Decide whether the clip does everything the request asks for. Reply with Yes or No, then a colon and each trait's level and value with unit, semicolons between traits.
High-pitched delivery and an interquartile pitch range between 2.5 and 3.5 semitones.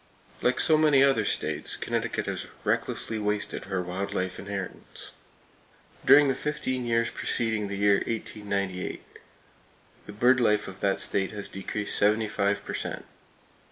No: low, 105 Hz; average, 3.2 semitones